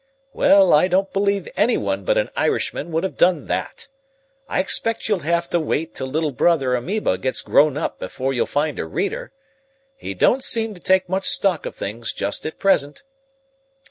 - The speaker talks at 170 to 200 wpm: Yes, average, 180 wpm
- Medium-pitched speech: Yes, medium, 170 Hz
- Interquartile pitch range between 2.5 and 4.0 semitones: No, average, 5.3 semitones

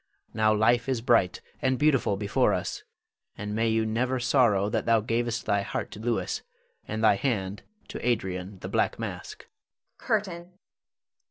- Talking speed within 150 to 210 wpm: Yes, average, 155 wpm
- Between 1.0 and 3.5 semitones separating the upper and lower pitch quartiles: Yes, average, 3.0 semitones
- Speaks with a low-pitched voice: Yes, low, 115 Hz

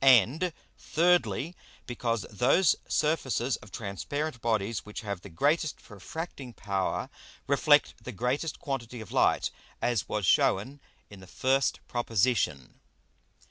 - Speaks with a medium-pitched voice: No, low, 120 Hz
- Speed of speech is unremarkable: No, slow, 120 wpm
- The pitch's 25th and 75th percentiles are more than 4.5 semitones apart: Yes, wide, 5.4 semitones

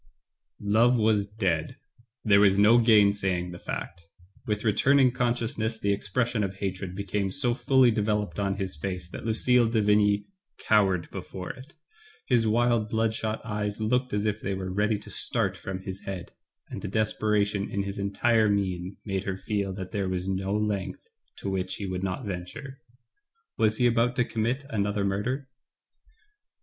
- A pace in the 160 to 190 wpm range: Yes, average, 165 wpm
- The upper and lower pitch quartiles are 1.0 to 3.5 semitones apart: Yes, average, 2.8 semitones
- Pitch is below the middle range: Yes, low, 105 Hz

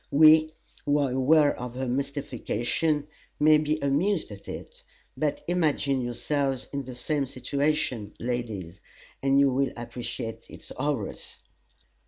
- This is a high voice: No, medium, 140 Hz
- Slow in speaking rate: Yes, slow, 130 wpm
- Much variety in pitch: No, average, 3.3 semitones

